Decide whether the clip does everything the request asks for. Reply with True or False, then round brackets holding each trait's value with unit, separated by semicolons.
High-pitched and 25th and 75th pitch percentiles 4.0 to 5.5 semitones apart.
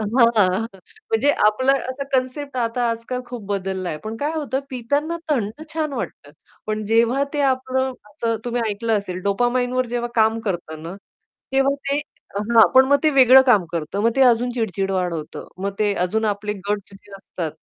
True (230 Hz; 4.4 semitones)